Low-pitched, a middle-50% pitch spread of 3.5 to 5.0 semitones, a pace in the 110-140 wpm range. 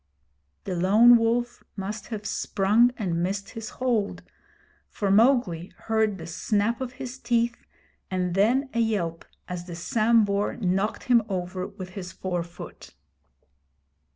No: high, 205 Hz; average, 4.2 semitones; slow, 135 wpm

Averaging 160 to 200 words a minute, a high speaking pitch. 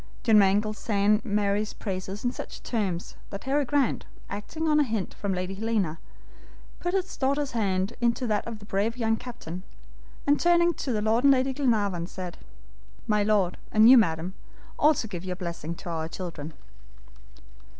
Yes: average, 165 wpm; high, 210 Hz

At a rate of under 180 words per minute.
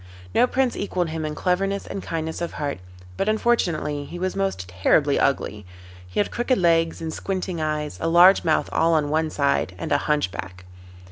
No: average, 185 wpm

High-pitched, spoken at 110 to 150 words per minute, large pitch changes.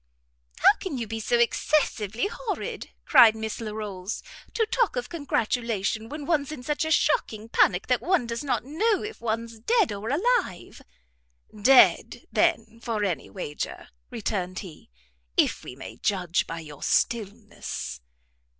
Yes: high, 230 Hz; average, 145 wpm; wide, 6.2 semitones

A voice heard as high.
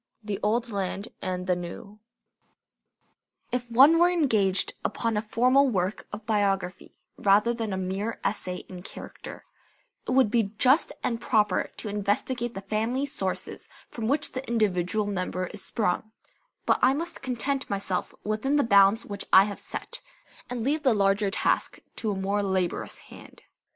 Yes: high, 210 Hz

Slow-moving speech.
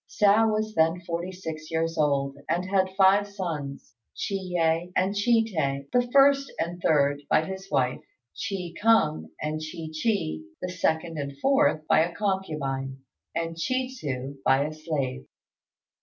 No: average, 155 wpm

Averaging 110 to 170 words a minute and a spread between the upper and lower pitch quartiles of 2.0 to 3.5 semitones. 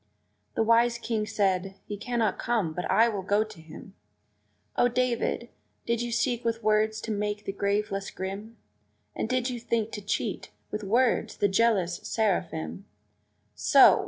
Yes: average, 160 wpm; average, 2.9 semitones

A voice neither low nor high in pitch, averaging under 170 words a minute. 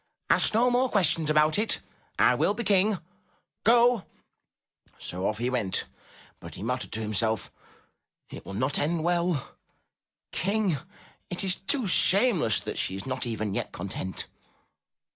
Yes: medium, 155 Hz; average, 160 wpm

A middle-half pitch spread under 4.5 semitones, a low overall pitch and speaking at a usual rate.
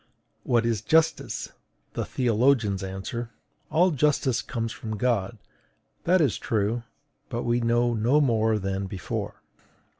No: average, 3.0 semitones; low, 115 Hz; slow, 125 wpm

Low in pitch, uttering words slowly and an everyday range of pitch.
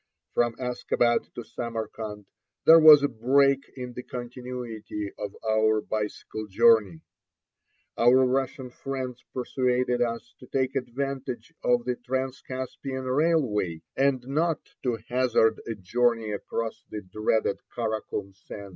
Yes: low, 120 Hz; slow, 125 wpm; average, 3.0 semitones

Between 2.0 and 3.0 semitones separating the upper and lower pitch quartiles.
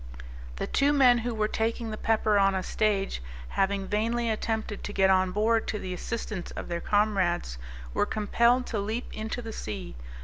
Yes: average, 2.7 semitones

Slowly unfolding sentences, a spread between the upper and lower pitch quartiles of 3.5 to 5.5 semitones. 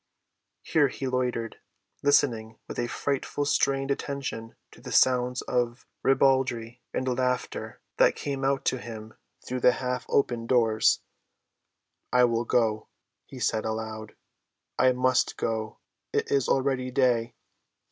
No: slow, 125 wpm; narrow, 2.5 semitones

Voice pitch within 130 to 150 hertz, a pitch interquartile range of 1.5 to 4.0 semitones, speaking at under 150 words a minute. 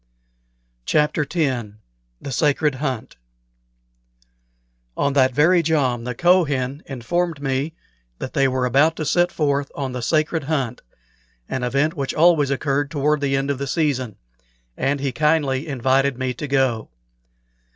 Yes: medium, 140 Hz; narrow, 2.6 semitones; average, 140 wpm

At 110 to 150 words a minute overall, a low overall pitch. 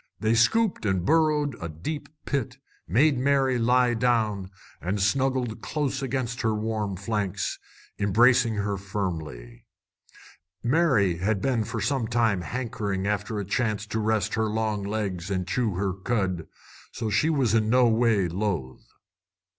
Yes: average, 145 wpm; low, 110 Hz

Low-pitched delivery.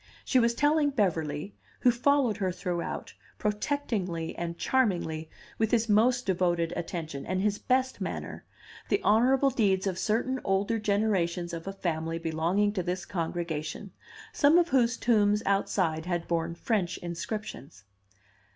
No: high, 195 Hz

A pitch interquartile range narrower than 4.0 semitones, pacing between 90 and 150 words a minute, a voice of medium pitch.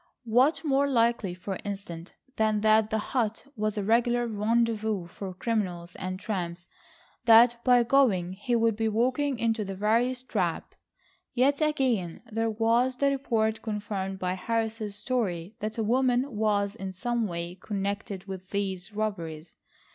No: average, 3.6 semitones; average, 145 wpm; high, 215 Hz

